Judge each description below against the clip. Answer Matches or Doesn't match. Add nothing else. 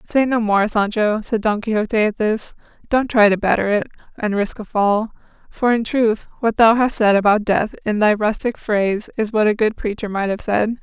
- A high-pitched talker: Matches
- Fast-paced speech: Matches